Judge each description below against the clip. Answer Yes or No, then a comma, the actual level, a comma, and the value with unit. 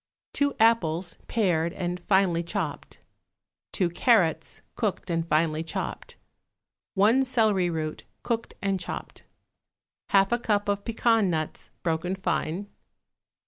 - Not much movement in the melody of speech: No, average, 4.6 semitones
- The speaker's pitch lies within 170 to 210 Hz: Yes, high, 190 Hz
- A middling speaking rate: No, slow, 115 wpm